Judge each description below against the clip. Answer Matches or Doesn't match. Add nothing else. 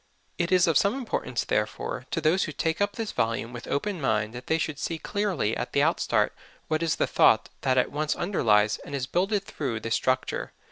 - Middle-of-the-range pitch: Matches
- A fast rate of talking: Matches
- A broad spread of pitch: Matches